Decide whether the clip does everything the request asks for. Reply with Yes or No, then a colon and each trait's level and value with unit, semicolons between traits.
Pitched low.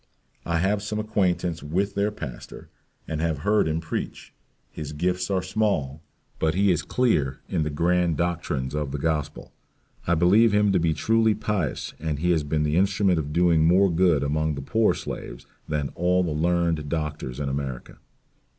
Yes: very low, 85 Hz